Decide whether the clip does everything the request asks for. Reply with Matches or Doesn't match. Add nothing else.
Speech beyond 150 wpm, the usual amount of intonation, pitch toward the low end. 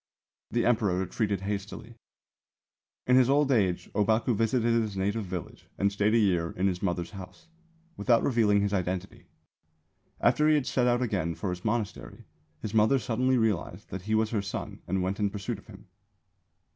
Matches